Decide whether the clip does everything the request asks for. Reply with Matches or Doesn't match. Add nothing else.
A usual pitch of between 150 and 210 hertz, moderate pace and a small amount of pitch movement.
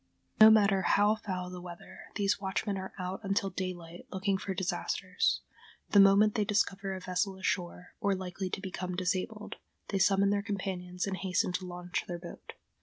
Matches